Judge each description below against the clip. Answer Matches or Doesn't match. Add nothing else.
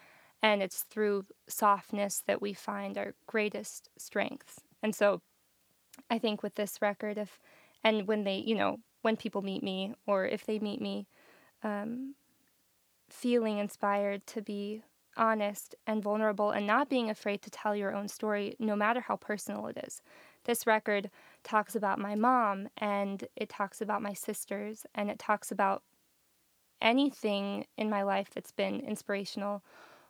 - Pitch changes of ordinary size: Doesn't match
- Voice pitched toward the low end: Doesn't match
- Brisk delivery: Doesn't match